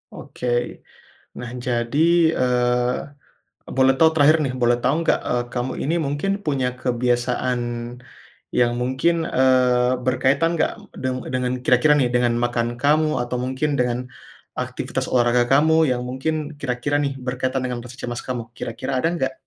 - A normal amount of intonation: No, narrow, 2.0 semitones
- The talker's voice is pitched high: No, low, 125 Hz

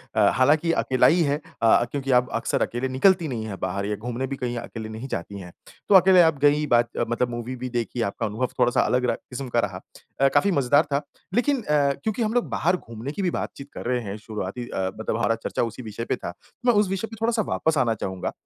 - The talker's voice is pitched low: Yes, low, 125 Hz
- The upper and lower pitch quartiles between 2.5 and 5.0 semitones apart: No, wide, 5.6 semitones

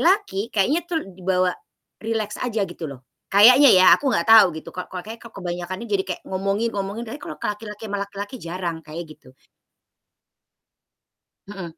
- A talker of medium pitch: No, high, 200 Hz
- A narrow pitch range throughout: No, average, 3.7 semitones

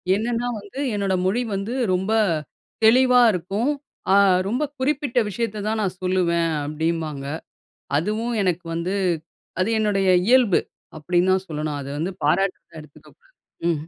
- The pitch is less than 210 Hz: Yes, high, 190 Hz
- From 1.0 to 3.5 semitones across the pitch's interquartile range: No, average, 5.1 semitones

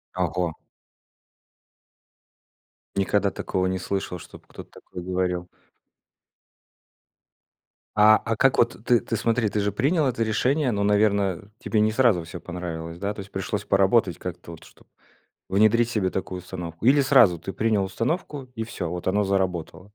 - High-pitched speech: No, low, 100 Hz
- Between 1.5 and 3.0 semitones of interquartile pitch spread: No, average, 3.8 semitones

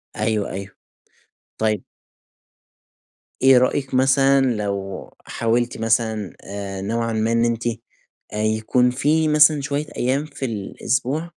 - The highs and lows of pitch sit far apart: No, average, 3.7 semitones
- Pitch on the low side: Yes, low, 115 Hz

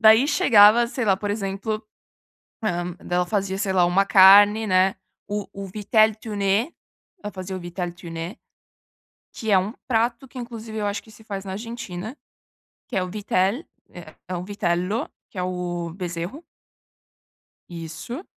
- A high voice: Yes, high, 200 Hz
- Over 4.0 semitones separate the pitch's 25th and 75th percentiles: No, average, 3.2 semitones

